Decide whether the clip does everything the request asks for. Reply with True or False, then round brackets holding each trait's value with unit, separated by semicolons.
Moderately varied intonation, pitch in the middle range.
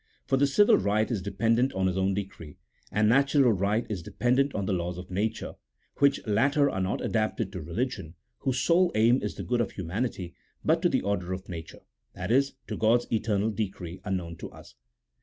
False (4.8 semitones; 105 Hz)